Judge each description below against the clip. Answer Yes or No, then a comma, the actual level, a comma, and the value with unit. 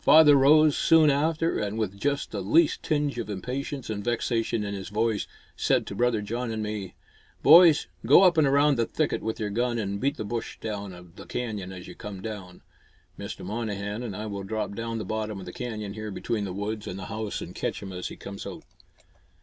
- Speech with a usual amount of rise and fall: Yes, average, 4.6 semitones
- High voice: No, low, 110 Hz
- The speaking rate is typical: No, fast, 220 wpm